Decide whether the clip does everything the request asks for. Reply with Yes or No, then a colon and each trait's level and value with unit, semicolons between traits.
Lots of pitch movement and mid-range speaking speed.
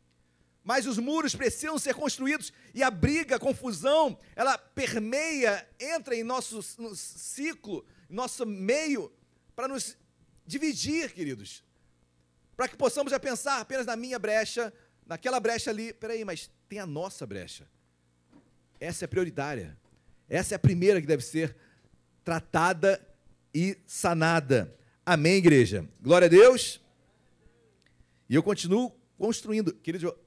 Yes: wide, 8.3 semitones; average, 130 wpm